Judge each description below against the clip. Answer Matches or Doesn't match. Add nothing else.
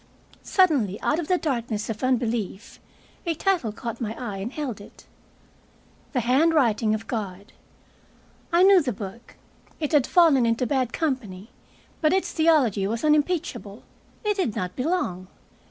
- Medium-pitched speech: Doesn't match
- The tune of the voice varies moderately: Doesn't match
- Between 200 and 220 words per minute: Doesn't match